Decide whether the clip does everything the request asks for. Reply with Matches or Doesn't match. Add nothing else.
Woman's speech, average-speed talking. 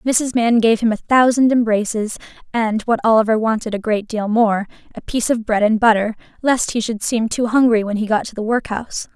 Doesn't match